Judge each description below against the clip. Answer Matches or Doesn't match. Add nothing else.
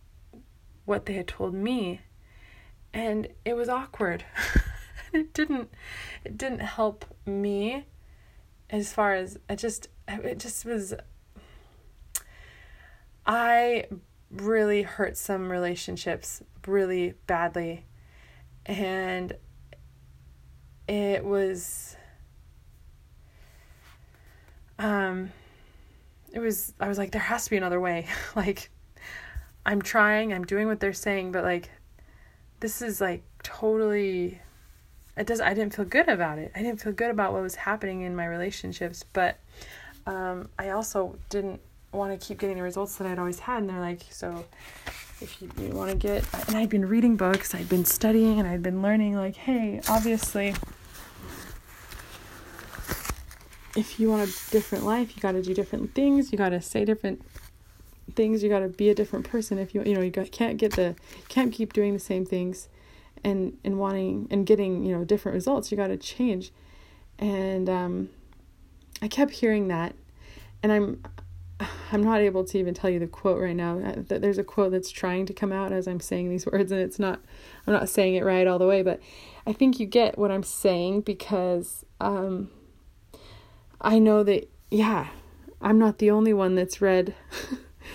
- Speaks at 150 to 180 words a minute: Matches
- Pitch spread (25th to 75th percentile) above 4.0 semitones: Doesn't match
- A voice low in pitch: Doesn't match